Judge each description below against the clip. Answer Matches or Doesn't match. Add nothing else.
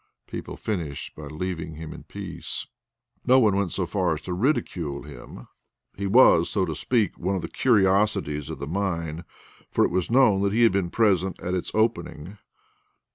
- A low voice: Matches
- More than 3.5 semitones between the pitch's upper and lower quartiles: Matches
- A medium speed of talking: Matches